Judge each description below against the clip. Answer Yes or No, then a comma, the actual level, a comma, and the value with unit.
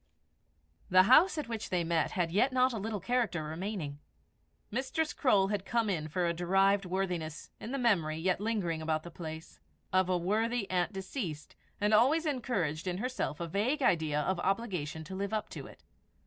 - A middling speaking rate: Yes, average, 185 wpm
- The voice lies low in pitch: No, high, 190 Hz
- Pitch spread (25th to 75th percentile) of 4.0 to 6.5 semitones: Yes, average, 5.2 semitones